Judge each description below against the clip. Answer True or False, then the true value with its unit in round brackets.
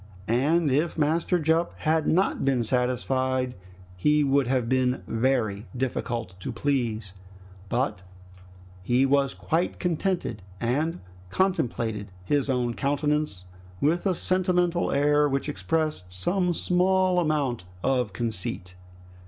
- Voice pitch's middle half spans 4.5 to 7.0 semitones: True (5.2 semitones)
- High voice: False (135 Hz)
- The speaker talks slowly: True (115 wpm)